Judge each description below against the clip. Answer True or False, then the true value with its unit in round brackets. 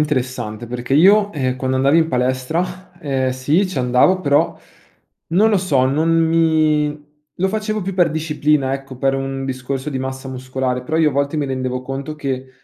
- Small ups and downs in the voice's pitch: False (3.7 semitones)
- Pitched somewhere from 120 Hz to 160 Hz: True (140 Hz)